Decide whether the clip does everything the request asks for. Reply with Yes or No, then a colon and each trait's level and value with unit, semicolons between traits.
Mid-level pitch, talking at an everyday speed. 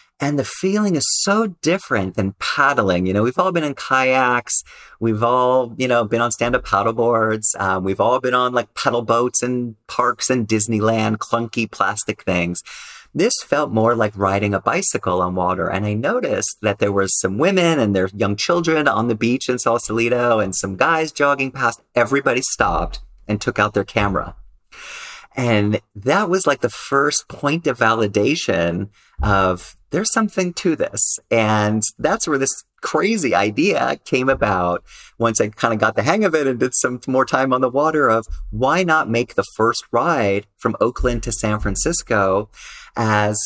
No: low, 115 Hz; average, 180 wpm